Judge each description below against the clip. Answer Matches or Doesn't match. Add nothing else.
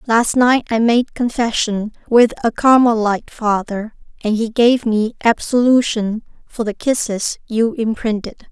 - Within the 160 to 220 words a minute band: Doesn't match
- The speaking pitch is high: Matches